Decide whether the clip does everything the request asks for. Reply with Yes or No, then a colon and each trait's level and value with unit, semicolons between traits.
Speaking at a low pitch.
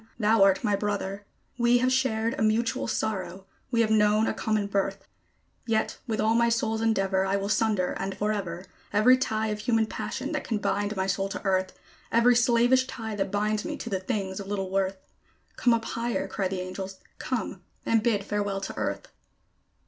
No: high, 210 Hz